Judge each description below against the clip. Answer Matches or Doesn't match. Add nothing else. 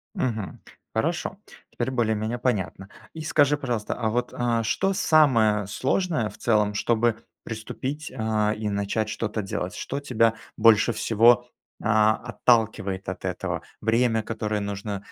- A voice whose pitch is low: Matches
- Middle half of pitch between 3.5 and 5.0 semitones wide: Doesn't match